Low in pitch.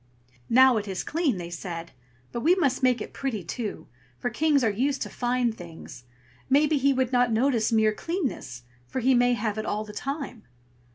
No: high, 245 Hz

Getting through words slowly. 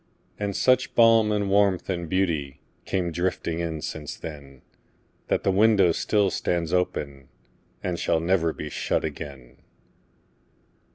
Yes: slow, 115 wpm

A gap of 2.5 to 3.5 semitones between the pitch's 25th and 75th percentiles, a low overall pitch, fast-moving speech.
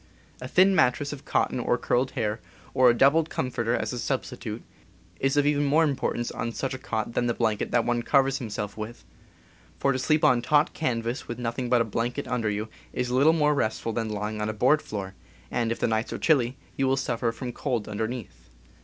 Yes: average, 3.1 semitones; low, 125 Hz; fast, 215 wpm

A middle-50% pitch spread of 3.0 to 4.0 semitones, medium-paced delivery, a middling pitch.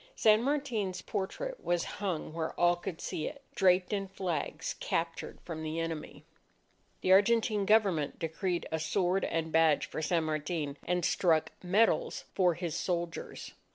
Yes: average, 3.5 semitones; average, 150 wpm; medium, 175 Hz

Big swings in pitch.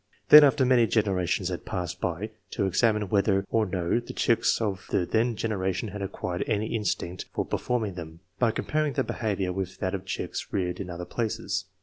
No: average, 3.7 semitones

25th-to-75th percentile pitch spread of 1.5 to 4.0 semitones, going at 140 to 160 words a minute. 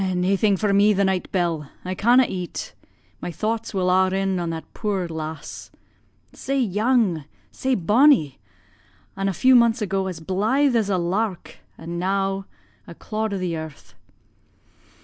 Yes: average, 3.5 semitones; average, 155 wpm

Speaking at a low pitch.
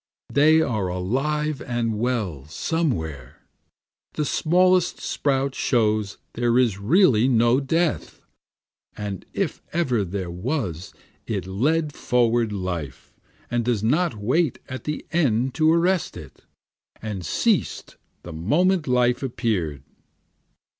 Yes: low, 120 Hz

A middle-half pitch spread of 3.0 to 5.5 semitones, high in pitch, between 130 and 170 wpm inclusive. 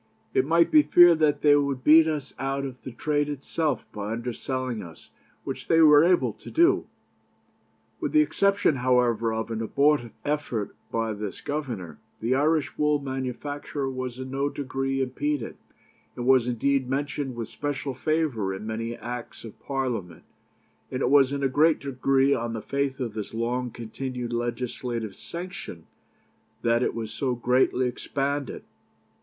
No: average, 3.6 semitones; low, 130 Hz; average, 160 wpm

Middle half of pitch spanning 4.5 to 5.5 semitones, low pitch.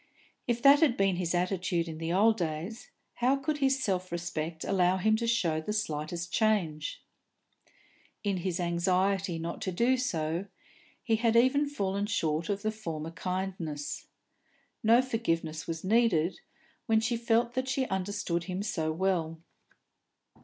No: average, 5.2 semitones; high, 190 Hz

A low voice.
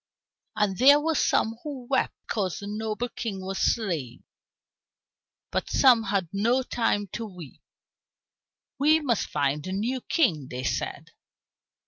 No: high, 215 Hz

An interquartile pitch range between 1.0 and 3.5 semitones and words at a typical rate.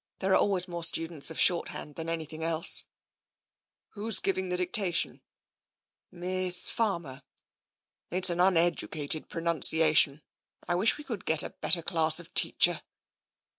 Yes: narrow, 2.4 semitones; average, 150 wpm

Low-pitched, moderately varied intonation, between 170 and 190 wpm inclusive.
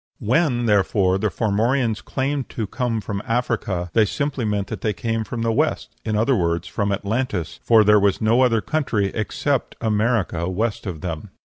Yes: low, 110 Hz; average, 3.3 semitones; average, 175 wpm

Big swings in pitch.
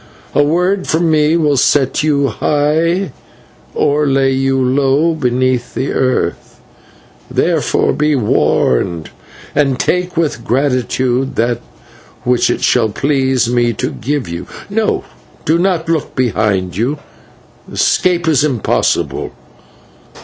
No: average, 3.9 semitones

